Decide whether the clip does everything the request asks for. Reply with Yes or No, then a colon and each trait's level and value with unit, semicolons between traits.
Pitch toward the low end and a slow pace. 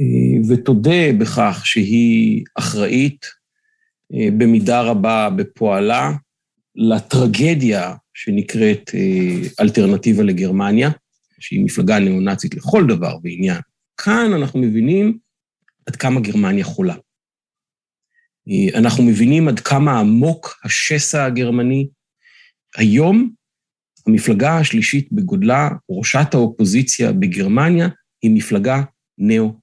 No: medium, 150 Hz; slow, 85 wpm